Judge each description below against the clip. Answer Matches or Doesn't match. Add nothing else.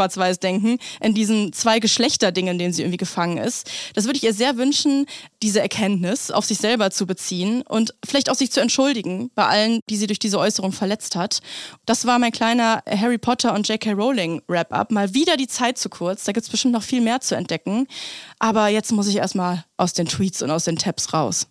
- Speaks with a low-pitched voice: Doesn't match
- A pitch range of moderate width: Matches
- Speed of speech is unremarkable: Doesn't match